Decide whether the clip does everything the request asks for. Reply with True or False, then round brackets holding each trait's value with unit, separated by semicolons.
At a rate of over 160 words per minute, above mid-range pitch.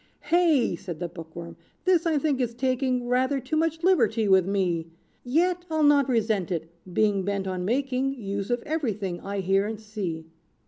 True (180 wpm; 225 Hz)